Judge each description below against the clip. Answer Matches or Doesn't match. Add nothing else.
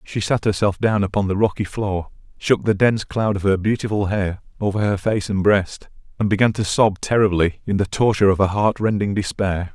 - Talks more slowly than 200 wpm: Doesn't match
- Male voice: Matches